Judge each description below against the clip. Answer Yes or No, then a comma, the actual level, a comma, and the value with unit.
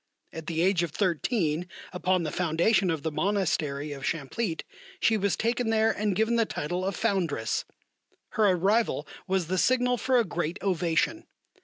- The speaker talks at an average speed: Yes, average, 165 wpm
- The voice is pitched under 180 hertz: No, medium, 185 Hz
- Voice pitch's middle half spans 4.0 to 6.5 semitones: Yes, average, 5.1 semitones